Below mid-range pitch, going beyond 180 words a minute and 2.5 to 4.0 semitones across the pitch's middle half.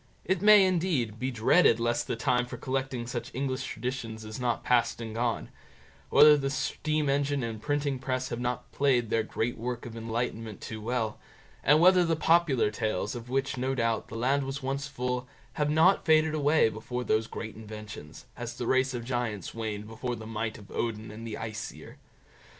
Yes: low, 125 Hz; average, 190 wpm; average, 3.5 semitones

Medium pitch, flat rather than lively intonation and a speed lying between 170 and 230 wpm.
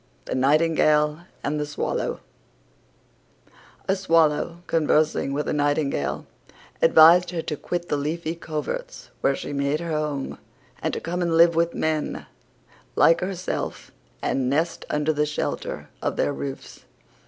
No: medium, 155 Hz; narrow, 2.3 semitones; average, 140 wpm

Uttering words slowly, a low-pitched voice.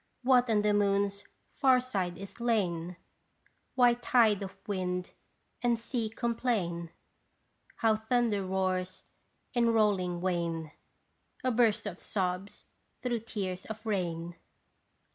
No: slow, 115 wpm; high, 205 Hz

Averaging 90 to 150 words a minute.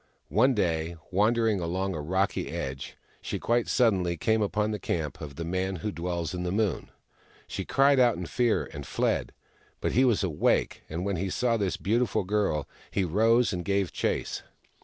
No: average, 180 wpm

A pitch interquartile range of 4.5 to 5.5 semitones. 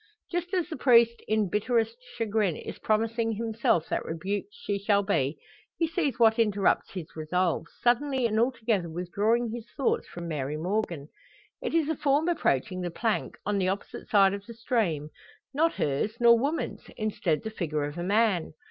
Yes: average, 4.8 semitones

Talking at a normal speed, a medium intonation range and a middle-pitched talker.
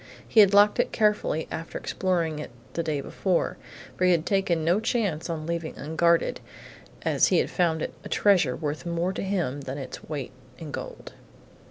Yes: average, 180 wpm; average, 3.5 semitones; medium, 170 Hz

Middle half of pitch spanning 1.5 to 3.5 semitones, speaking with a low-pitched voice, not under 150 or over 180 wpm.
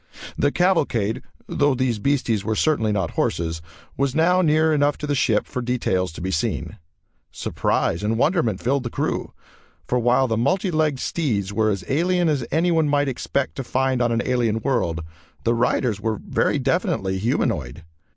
No: average, 5.2 semitones; low, 125 Hz; average, 170 wpm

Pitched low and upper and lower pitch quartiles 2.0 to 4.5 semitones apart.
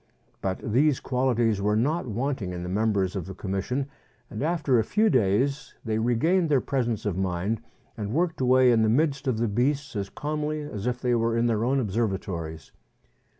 No: low, 120 Hz; average, 5.1 semitones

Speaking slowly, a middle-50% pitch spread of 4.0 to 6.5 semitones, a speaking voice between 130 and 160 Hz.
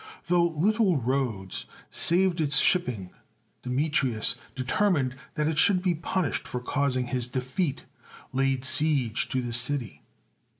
Yes: slow, 130 wpm; average, 5.1 semitones; low, 135 Hz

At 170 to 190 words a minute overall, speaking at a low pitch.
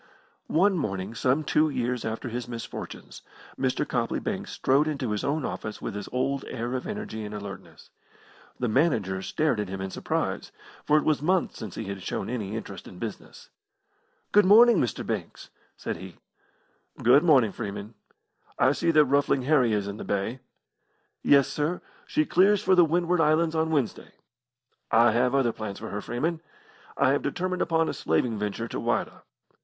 Yes: average, 175 wpm; low, 130 Hz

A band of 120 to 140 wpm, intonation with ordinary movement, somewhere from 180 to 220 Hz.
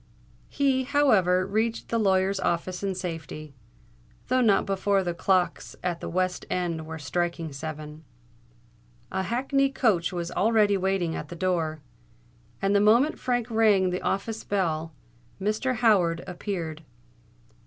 Yes: slow, 135 wpm; average, 4.3 semitones; high, 190 Hz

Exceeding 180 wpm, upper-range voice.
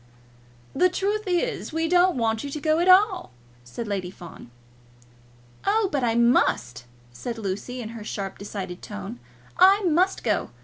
No: average, 160 wpm; very high, 250 Hz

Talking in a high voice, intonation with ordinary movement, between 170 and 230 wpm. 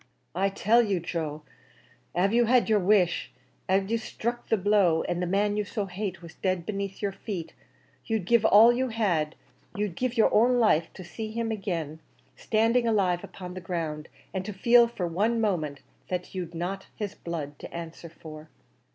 Yes: high, 195 Hz; average, 4.3 semitones; average, 185 wpm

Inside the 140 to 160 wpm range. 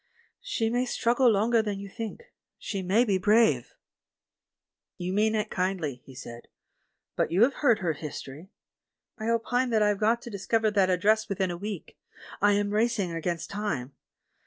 No: average, 175 wpm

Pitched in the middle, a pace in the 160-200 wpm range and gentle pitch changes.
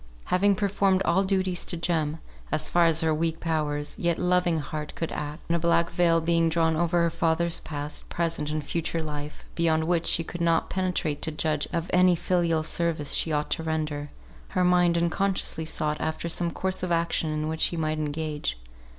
Yes: medium, 165 Hz; average, 195 wpm; narrow, 1.8 semitones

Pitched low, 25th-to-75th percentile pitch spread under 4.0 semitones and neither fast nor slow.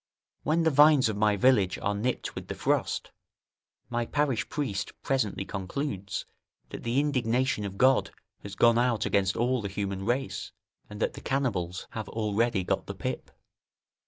No: low, 115 Hz; average, 4.6 semitones; average, 160 wpm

